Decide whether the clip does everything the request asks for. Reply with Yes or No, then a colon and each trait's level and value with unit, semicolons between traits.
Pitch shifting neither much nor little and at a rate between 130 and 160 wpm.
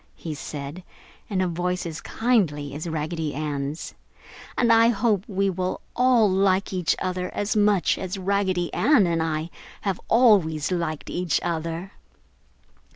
Yes: average, 3.7 semitones; average, 145 wpm